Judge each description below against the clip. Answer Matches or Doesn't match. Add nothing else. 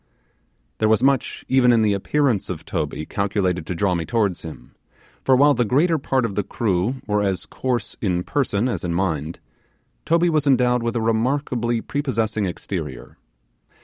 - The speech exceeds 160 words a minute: Matches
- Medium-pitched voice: Doesn't match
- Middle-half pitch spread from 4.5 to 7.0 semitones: Matches